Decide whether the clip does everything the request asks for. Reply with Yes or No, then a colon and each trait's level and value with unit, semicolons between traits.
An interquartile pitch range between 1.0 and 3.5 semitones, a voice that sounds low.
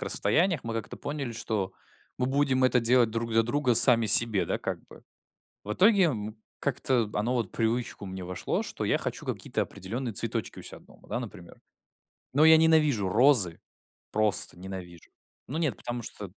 No: average, 4.3 semitones; low, 115 Hz